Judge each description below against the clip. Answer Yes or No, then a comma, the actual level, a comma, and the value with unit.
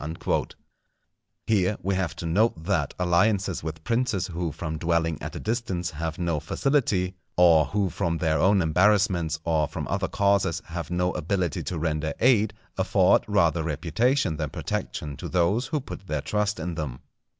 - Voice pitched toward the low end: Yes, very low, 90 Hz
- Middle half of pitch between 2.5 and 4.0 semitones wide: Yes, average, 3.7 semitones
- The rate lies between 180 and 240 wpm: No, average, 165 wpm